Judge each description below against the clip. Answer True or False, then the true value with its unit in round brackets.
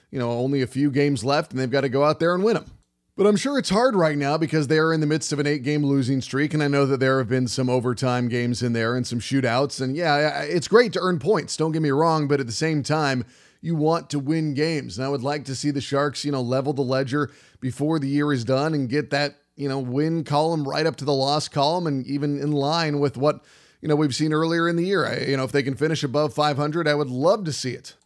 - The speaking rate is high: True (280 wpm)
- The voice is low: False (145 Hz)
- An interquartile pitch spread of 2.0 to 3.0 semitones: True (2.5 semitones)